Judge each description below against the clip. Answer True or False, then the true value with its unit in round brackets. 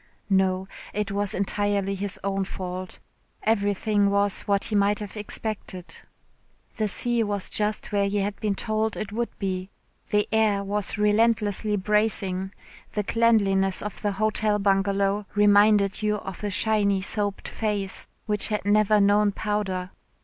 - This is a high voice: True (205 Hz)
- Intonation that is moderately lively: False (1.3 semitones)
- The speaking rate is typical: True (145 wpm)